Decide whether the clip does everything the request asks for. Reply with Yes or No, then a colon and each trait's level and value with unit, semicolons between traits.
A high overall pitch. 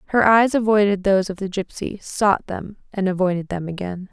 Yes: high, 195 Hz